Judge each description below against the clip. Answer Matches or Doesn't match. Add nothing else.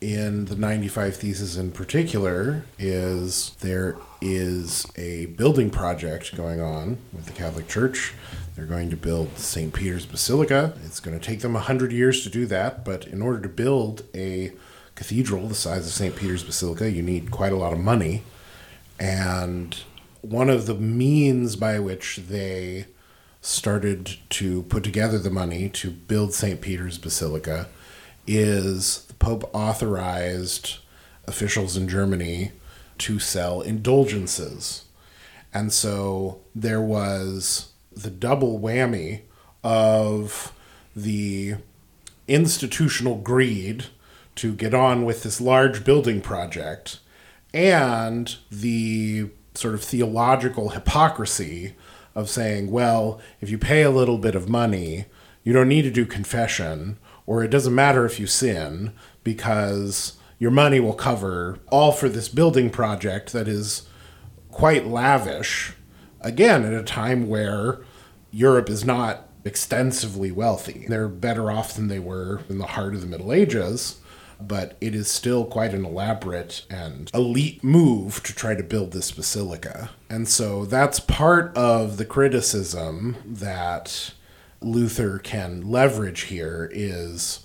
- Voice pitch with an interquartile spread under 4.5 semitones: Matches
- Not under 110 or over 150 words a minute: Matches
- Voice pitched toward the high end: Doesn't match